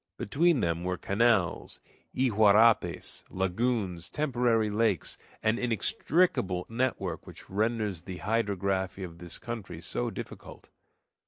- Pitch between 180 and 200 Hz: No, low, 105 Hz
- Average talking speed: No, slow, 105 wpm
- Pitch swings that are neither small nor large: Yes, average, 4.1 semitones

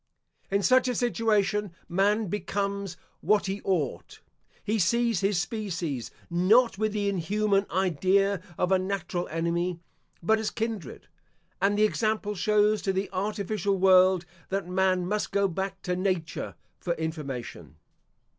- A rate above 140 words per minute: No, slow, 135 wpm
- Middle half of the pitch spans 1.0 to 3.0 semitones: Yes, average, 2.7 semitones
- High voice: Yes, high, 195 Hz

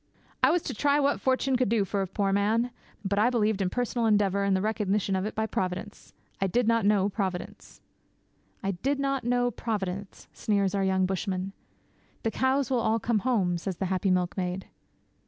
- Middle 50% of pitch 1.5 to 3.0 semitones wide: No, average, 3.7 semitones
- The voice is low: No, high, 205 Hz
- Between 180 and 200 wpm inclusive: Yes, average, 195 wpm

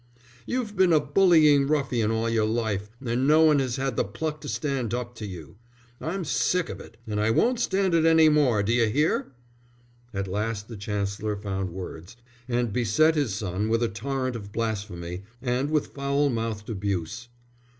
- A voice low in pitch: Yes, low, 120 Hz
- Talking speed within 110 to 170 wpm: No, average, 180 wpm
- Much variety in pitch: Yes, wide, 5.9 semitones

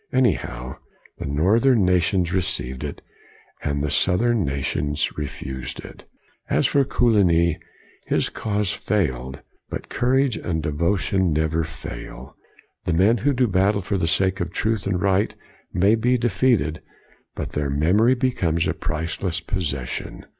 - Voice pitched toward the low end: Yes, very low, 90 Hz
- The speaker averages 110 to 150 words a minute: Yes, average, 140 wpm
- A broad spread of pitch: Yes, wide, 5.8 semitones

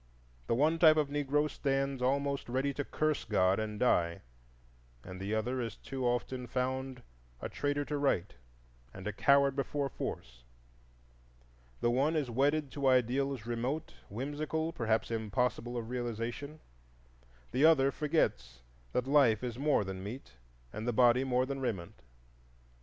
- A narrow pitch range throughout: No, average, 3.5 semitones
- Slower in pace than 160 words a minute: Yes, average, 145 wpm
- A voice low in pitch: Yes, low, 130 Hz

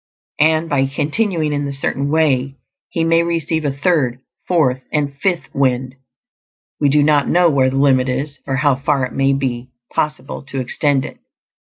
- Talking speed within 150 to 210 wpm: Yes, average, 175 wpm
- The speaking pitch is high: No, medium, 140 Hz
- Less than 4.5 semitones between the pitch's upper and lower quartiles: Yes, average, 2.7 semitones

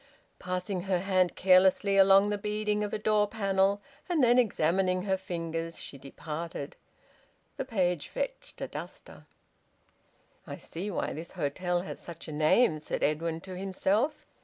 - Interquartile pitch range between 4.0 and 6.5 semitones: No, average, 3.6 semitones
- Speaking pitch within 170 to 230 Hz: Yes, high, 190 Hz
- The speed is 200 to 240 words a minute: No, average, 150 wpm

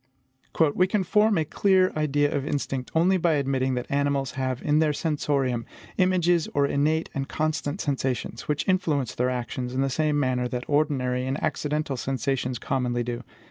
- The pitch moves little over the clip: No, average, 3.3 semitones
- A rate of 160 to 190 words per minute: Yes, average, 170 wpm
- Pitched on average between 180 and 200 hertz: No, medium, 140 Hz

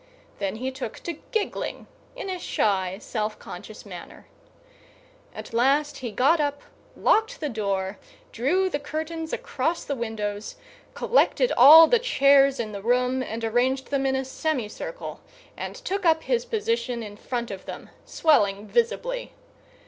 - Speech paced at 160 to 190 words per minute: No, average, 150 wpm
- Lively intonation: Yes, wide, 7.1 semitones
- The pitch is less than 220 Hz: No, very high, 270 Hz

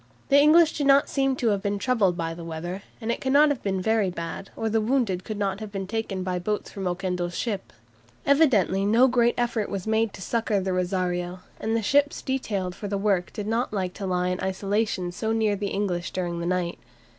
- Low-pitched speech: No, high, 200 Hz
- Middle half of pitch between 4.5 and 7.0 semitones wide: No, average, 3.7 semitones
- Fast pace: Yes, fast, 220 wpm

